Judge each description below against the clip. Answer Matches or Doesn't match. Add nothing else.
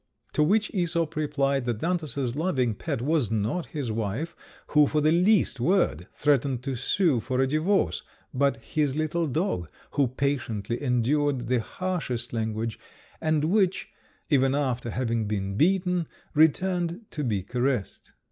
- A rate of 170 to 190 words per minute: Doesn't match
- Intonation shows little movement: Doesn't match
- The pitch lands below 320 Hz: Matches